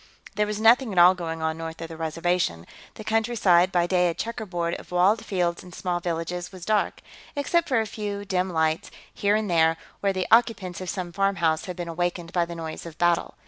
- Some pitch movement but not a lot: Yes, average, 3.2 semitones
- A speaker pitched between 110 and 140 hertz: No, medium, 180 Hz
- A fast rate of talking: Yes, fast, 210 wpm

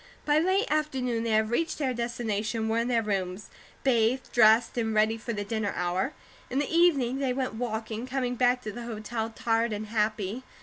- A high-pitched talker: Yes, high, 230 Hz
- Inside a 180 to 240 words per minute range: Yes, average, 200 wpm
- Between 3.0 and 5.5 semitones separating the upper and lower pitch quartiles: No, narrow, 2.6 semitones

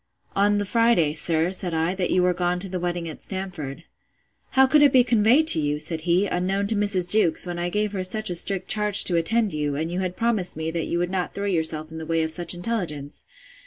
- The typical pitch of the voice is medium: Yes, medium, 180 Hz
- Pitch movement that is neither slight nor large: Yes, average, 3.7 semitones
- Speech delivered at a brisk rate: Yes, fast, 240 wpm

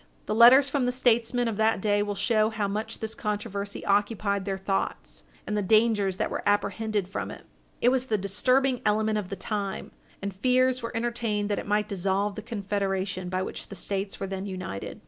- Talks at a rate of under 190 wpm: No, average, 200 wpm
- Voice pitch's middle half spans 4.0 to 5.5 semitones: No, narrow, 2.5 semitones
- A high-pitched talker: Yes, high, 210 Hz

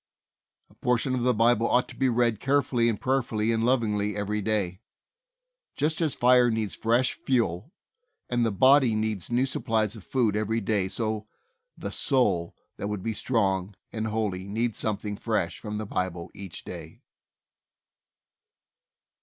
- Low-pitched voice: Yes, low, 110 Hz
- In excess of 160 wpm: No, average, 155 wpm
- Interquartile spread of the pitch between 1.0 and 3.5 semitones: Yes, average, 2.9 semitones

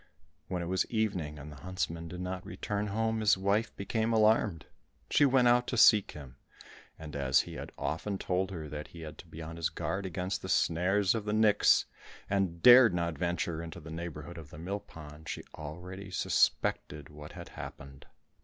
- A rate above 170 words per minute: Yes, average, 190 wpm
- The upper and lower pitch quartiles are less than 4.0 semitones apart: No, average, 4.6 semitones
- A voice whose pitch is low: Yes, very low, 90 Hz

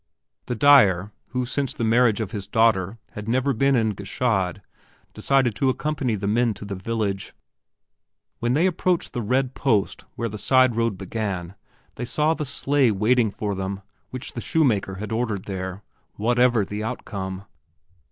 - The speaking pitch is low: Yes, low, 115 Hz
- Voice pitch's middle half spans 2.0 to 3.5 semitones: No, average, 4.1 semitones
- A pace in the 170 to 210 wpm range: No, average, 160 wpm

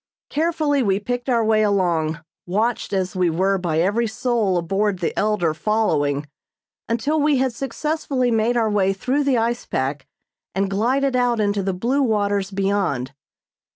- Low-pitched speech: No, high, 210 Hz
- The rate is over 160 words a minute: No, average, 155 wpm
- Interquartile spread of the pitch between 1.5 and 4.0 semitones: No, average, 4.5 semitones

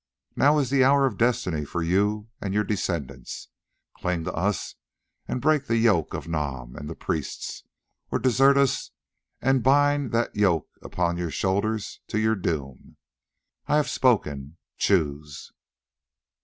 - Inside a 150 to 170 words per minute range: No, average, 140 wpm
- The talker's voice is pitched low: Yes, low, 100 Hz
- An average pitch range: No, wide, 7.7 semitones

